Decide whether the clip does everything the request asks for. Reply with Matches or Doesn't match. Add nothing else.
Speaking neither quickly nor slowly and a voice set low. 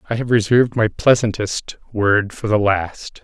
Matches